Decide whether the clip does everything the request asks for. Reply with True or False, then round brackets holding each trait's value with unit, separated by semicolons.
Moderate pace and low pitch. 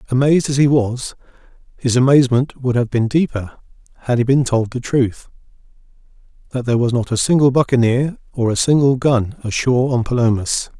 True (165 wpm; 125 Hz)